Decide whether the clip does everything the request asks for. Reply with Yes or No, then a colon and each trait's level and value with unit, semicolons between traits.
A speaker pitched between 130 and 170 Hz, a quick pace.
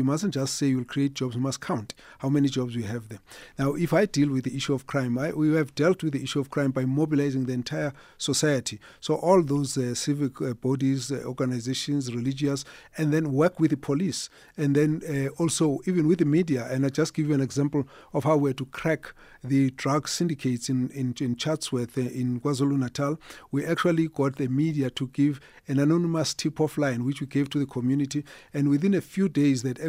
Yes: medium, 140 Hz; fast, 215 wpm